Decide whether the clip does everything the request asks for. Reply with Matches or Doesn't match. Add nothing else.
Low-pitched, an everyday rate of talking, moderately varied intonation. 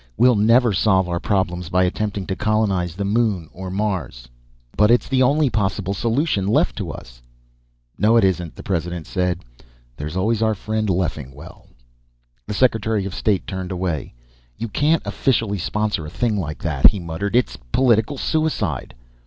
Matches